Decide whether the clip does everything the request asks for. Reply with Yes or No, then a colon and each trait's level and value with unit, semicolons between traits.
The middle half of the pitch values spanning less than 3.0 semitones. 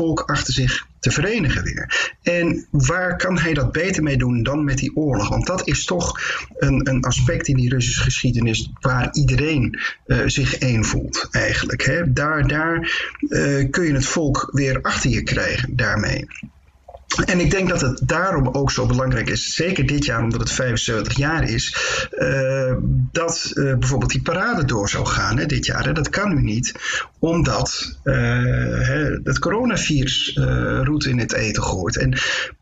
No: average, 3.4 semitones